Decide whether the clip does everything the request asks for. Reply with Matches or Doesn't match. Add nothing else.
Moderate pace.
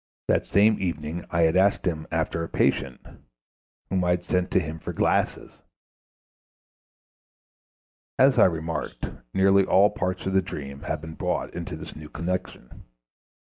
Matches